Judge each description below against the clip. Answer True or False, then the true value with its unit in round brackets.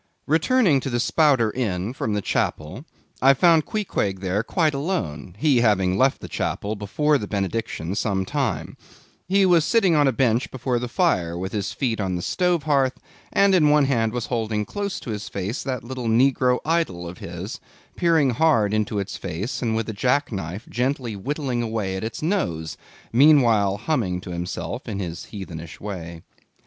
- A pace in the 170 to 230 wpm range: True (180 wpm)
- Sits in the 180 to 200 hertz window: False (115 Hz)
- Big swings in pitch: True (6.6 semitones)